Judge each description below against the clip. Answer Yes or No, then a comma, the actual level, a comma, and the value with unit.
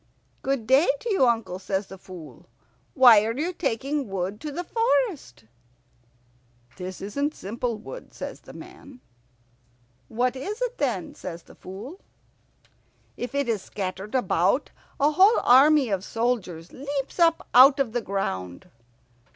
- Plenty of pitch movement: Yes, wide, 6.7 semitones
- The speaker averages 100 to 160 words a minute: Yes, average, 145 wpm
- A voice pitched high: Yes, high, 245 Hz